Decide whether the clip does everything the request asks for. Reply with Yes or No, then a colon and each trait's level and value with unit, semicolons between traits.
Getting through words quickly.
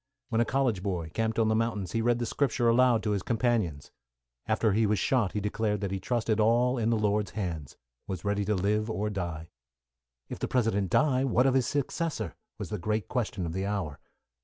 Yes: fast, 210 wpm